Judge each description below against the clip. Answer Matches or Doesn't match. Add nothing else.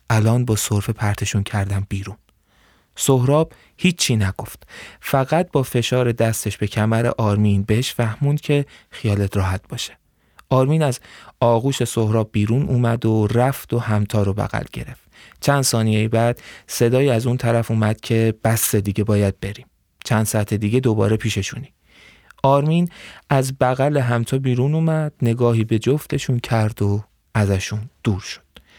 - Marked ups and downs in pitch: Doesn't match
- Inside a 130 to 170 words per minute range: Matches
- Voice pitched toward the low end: Matches